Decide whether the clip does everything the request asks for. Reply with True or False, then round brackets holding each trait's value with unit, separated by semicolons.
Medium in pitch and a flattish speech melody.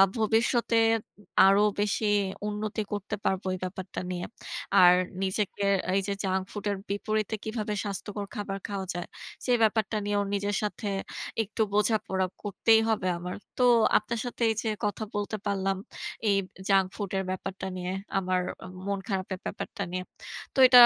False (205 Hz; 2.1 semitones)